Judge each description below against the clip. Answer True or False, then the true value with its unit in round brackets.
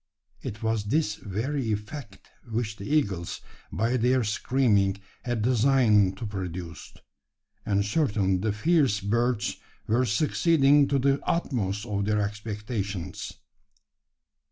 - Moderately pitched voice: False (110 Hz)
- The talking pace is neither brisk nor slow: False (115 wpm)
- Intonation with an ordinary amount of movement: True (4.2 semitones)